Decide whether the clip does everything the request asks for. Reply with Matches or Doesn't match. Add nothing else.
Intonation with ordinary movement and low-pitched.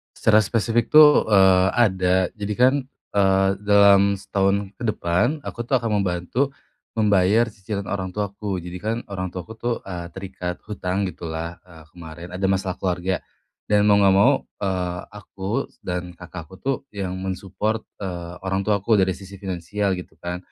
Doesn't match